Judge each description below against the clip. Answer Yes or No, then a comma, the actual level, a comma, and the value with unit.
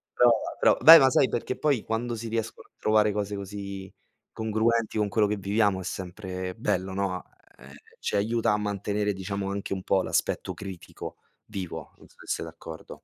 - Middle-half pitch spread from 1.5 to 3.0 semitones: Yes, narrow, 2.5 semitones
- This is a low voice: Yes, low, 100 Hz